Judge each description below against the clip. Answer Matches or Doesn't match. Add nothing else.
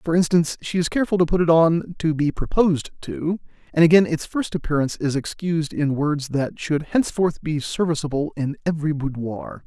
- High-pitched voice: Doesn't match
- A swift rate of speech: Doesn't match